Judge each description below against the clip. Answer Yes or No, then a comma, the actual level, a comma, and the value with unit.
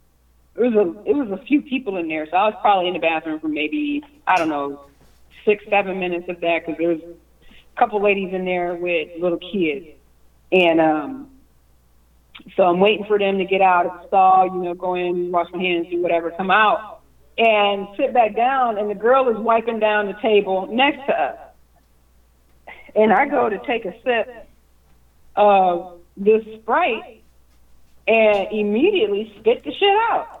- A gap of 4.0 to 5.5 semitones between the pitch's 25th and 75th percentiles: Yes, average, 5.2 semitones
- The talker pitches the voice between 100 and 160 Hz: No, medium, 185 Hz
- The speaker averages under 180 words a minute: No, average, 185 wpm